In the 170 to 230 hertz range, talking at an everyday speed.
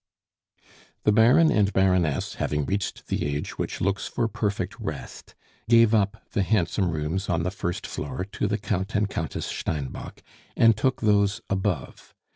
No: low, 100 Hz; average, 155 wpm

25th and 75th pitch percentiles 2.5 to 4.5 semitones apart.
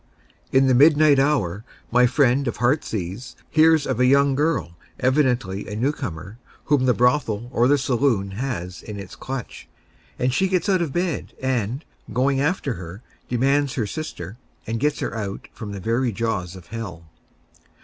No: average, 4.9 semitones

